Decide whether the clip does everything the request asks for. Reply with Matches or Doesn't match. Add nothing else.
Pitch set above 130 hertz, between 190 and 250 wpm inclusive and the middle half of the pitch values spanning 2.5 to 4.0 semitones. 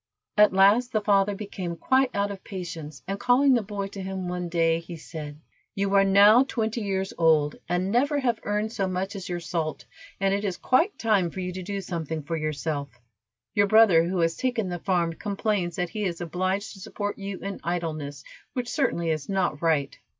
Matches